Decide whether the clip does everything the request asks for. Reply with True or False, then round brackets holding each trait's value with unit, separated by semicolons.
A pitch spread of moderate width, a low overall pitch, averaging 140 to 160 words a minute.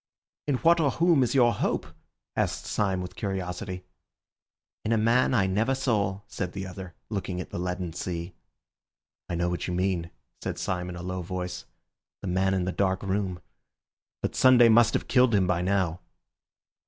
False (3.8 semitones; 95 Hz; 180 wpm)